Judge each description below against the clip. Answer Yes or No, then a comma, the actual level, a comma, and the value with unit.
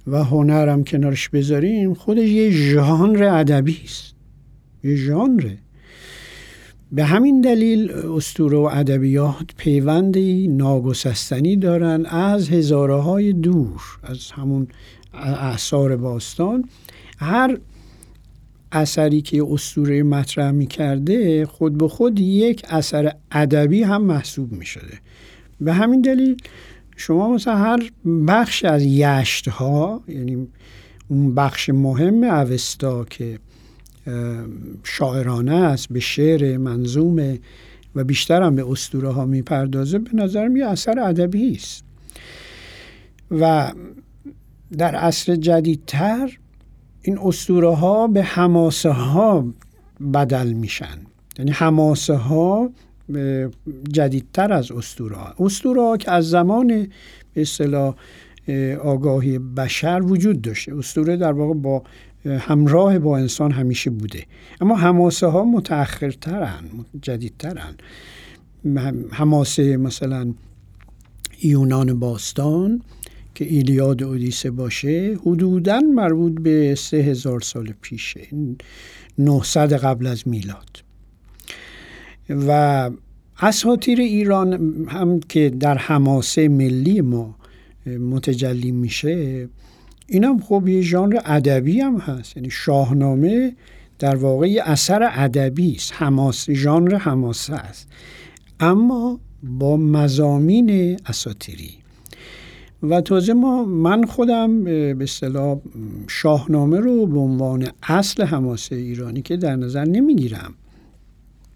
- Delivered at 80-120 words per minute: Yes, slow, 105 wpm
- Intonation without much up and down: No, average, 5.2 semitones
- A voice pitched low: No, medium, 145 Hz